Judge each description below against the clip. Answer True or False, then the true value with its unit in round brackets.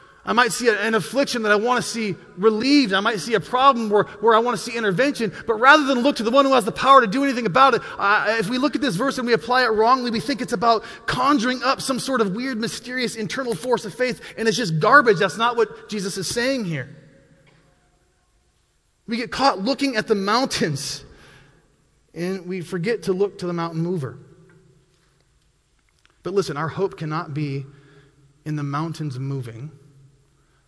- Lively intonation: True (6.8 semitones)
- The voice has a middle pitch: False (215 Hz)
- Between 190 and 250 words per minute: True (200 wpm)